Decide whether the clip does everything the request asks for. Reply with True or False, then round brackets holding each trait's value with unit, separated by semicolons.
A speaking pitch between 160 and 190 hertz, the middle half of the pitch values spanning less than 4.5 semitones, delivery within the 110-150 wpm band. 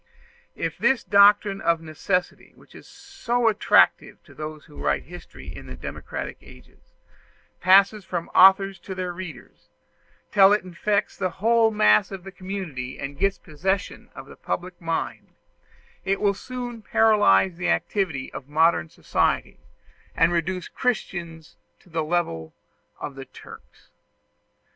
True (185 Hz; 3.7 semitones; 140 wpm)